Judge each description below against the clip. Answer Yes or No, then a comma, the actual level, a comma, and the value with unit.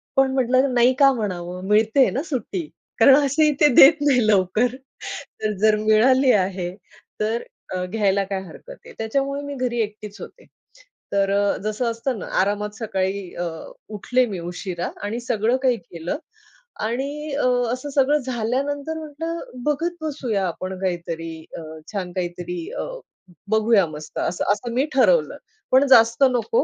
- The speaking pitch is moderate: No, high, 230 Hz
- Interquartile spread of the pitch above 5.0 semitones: Yes, wide, 5.5 semitones